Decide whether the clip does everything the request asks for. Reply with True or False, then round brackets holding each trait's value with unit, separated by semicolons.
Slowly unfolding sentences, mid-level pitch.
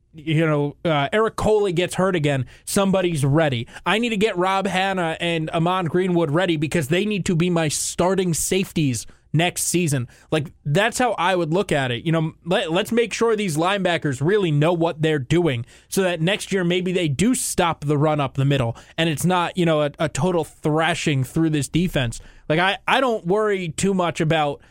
False (205 wpm; 170 Hz)